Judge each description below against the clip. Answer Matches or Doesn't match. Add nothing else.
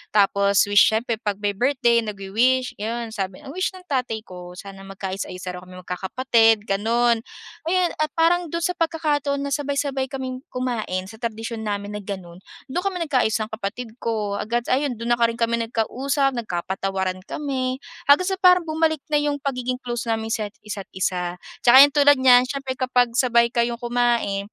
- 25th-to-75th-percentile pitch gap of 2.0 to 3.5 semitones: Doesn't match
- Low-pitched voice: Doesn't match